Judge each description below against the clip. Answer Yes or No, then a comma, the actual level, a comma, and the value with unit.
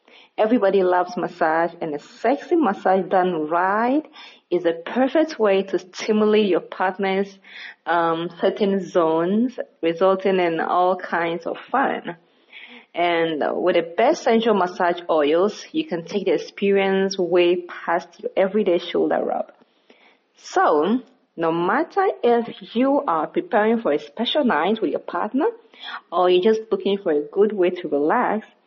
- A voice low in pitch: No, high, 195 Hz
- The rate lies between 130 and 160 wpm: Yes, average, 140 wpm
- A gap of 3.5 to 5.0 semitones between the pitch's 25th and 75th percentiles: Yes, average, 4.6 semitones